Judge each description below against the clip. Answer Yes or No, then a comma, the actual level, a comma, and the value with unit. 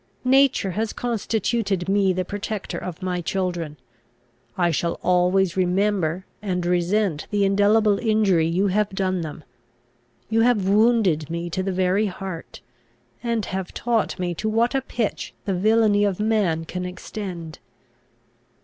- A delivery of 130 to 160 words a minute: Yes, average, 140 wpm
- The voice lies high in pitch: Yes, high, 195 Hz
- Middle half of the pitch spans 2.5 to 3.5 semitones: Yes, average, 3.2 semitones